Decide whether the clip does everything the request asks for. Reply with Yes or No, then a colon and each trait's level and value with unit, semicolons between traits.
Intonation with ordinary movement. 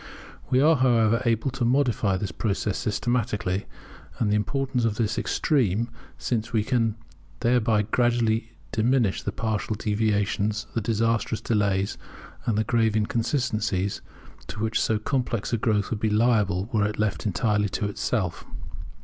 No: narrow, 2.3 semitones